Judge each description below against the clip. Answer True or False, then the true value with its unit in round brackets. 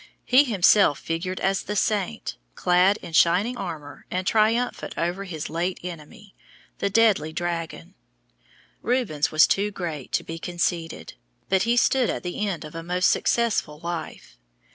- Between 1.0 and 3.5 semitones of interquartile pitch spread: False (4.0 semitones)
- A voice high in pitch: False (180 Hz)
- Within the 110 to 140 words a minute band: False (150 wpm)